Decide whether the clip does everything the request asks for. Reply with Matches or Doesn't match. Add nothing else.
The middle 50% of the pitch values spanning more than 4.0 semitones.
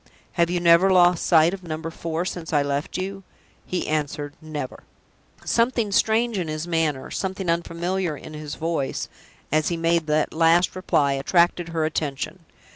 Doesn't match